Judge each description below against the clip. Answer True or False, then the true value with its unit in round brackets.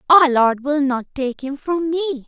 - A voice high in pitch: True (285 Hz)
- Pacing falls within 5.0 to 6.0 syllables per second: False (4.7 syllables/s)